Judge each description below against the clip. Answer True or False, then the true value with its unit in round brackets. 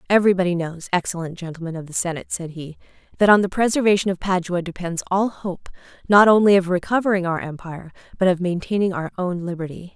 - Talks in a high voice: False (180 Hz)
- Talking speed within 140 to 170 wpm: False (180 wpm)